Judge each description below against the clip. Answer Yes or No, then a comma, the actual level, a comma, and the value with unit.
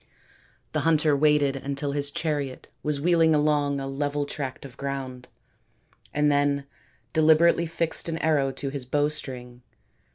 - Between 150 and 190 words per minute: No, slow, 135 wpm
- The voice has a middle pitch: Yes, medium, 145 Hz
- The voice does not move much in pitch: Yes, narrow, 1.8 semitones